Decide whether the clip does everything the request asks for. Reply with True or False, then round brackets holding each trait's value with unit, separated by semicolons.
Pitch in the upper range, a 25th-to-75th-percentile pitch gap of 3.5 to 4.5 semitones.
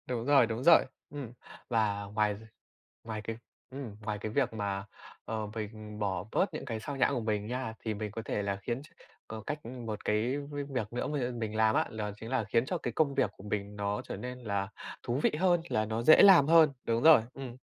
False (115 Hz; 4.0 semitones)